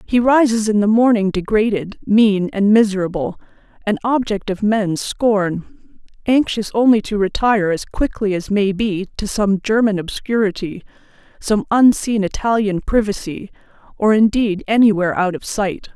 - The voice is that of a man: No, female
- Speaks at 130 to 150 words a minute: Yes, average, 140 wpm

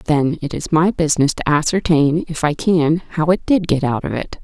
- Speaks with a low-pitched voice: No, medium, 160 Hz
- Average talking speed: No, fast, 230 wpm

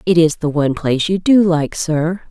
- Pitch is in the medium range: Yes, medium, 165 Hz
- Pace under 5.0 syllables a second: No, 5.2 syllables/s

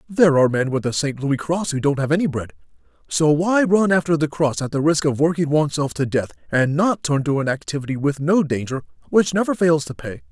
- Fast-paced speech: Yes, fast, 240 wpm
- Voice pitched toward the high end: No, medium, 145 Hz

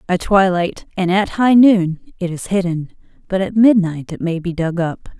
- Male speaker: No, female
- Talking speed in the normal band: Yes, average, 195 wpm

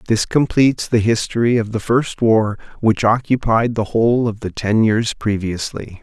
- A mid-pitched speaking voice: No, low, 110 Hz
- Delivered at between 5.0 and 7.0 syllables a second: No, 4.6 syllables/s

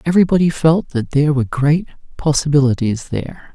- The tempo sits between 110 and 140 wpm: Yes, slow, 135 wpm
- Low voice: No, medium, 145 Hz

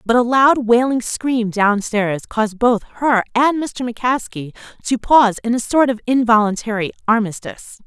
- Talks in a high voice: Yes, high, 230 Hz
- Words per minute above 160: No, average, 155 wpm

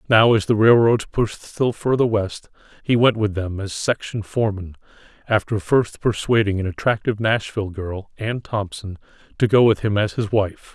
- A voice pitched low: Yes, low, 105 Hz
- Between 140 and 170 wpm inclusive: Yes, average, 165 wpm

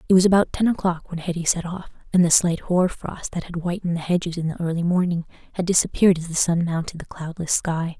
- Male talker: No, female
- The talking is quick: Yes, fast, 240 wpm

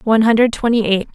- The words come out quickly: Yes, fast, 210 wpm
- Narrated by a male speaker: No, female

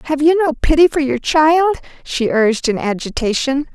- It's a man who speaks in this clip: No, female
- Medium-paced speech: Yes, average, 175 wpm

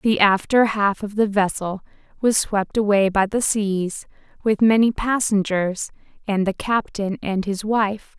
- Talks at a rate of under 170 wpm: Yes, average, 155 wpm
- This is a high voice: Yes, high, 205 Hz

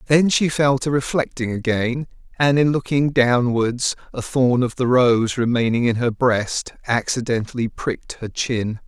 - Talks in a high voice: No, low, 125 Hz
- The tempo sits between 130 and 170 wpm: Yes, average, 155 wpm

